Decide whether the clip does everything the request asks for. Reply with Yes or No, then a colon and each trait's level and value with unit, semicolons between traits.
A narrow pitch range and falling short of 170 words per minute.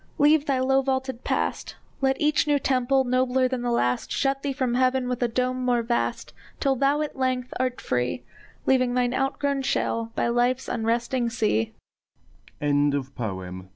Yes: narrow, 1.8 semitones; average, 155 wpm